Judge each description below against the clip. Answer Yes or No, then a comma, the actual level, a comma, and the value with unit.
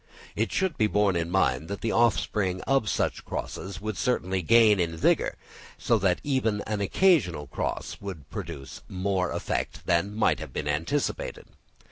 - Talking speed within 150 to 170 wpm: Yes, average, 160 wpm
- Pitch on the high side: No, low, 100 Hz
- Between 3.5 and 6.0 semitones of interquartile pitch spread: Yes, average, 4.2 semitones